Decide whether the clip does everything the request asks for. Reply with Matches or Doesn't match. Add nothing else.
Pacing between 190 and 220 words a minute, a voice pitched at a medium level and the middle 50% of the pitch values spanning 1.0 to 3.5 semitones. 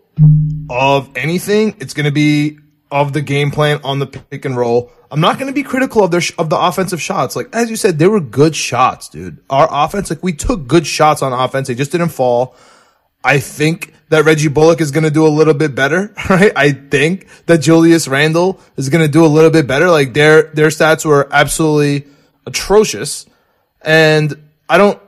Matches